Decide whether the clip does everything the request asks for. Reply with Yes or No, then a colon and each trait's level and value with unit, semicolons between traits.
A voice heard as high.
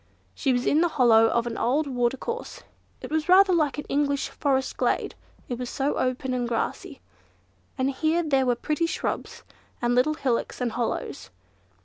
Yes: very high, 265 Hz